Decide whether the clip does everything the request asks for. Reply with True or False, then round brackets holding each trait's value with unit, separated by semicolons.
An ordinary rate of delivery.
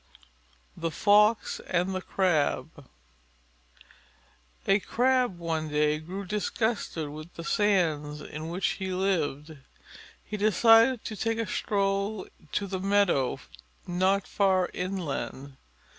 False (115 wpm)